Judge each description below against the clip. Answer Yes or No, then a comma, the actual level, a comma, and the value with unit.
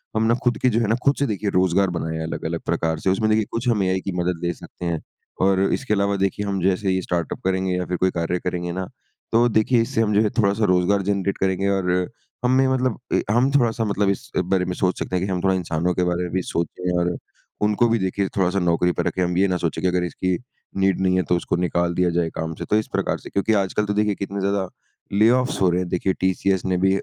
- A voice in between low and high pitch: No, very low, 95 Hz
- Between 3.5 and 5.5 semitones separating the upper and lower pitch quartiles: No, average, 2.7 semitones